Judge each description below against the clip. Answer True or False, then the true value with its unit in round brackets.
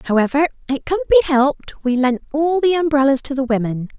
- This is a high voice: True (280 Hz)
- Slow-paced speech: False (195 wpm)